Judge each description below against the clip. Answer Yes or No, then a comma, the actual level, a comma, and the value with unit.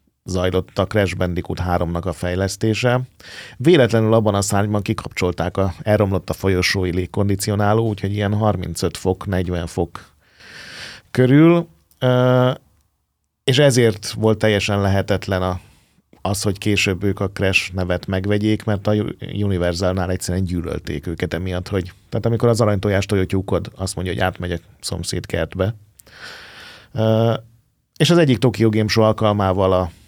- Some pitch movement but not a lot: Yes, average, 3.2 semitones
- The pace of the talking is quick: No, average, 130 wpm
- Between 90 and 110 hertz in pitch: Yes, low, 100 Hz